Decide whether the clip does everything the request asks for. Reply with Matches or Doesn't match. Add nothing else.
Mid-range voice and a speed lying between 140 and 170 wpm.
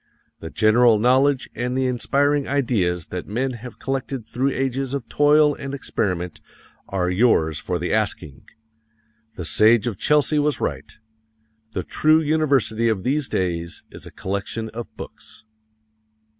Doesn't match